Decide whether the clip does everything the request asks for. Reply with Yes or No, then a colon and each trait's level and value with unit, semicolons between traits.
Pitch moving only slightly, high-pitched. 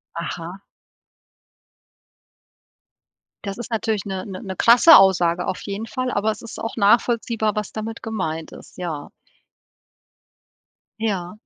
No: average, 3.4 semitones; high, 205 Hz